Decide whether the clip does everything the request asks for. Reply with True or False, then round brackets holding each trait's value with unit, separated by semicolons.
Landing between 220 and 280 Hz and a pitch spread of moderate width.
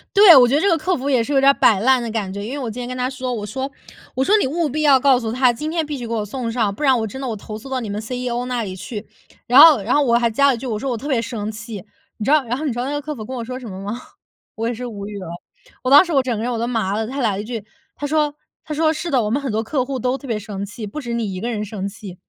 True (245 Hz; 3.9 semitones)